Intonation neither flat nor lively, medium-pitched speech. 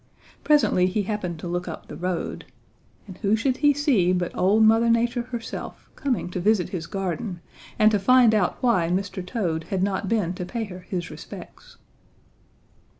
No: average, 4.2 semitones; high, 195 Hz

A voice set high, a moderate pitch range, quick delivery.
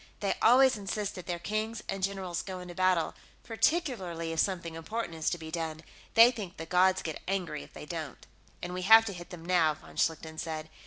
No: medium, 180 Hz; average, 3.9 semitones; fast, 210 wpm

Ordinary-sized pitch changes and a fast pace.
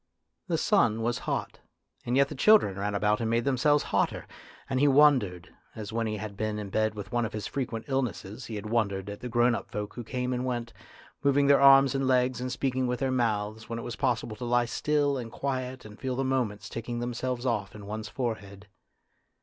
Yes: average, 3.3 semitones; fast, 220 wpm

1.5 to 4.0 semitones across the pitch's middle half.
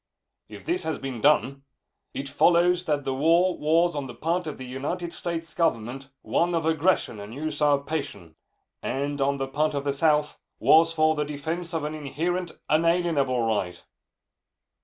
Yes: average, 3.4 semitones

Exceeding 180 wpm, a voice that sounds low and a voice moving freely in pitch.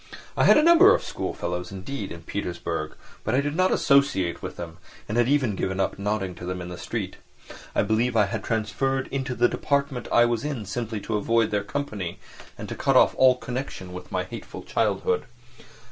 Yes: average, 200 wpm; low, 110 Hz; wide, 5.8 semitones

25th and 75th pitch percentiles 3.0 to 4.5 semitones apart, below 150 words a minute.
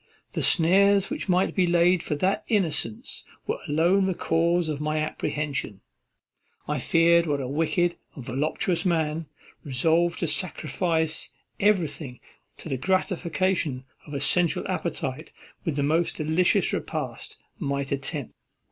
Yes: average, 3.4 semitones; slow, 135 wpm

